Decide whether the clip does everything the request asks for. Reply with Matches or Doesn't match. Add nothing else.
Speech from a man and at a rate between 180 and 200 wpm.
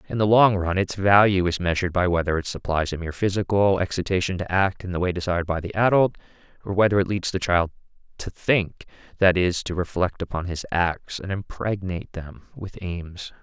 Matches